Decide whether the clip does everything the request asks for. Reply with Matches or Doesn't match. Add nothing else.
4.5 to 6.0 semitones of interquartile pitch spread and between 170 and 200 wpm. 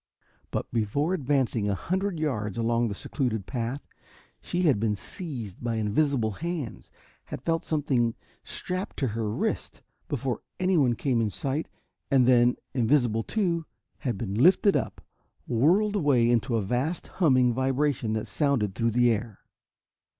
Doesn't match